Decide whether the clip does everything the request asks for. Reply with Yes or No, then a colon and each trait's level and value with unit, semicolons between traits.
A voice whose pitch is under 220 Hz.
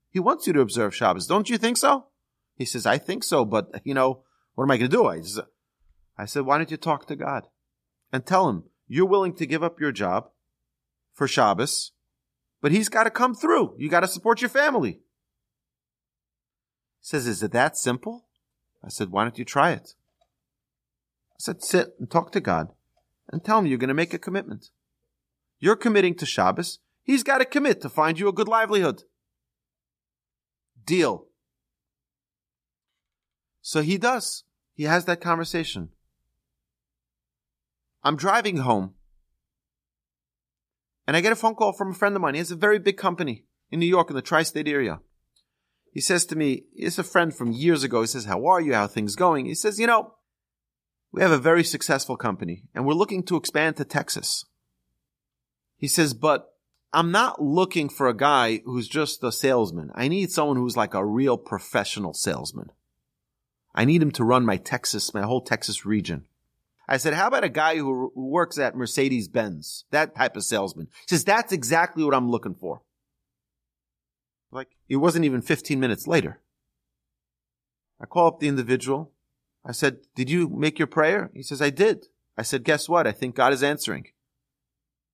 Yes: medium, 140 Hz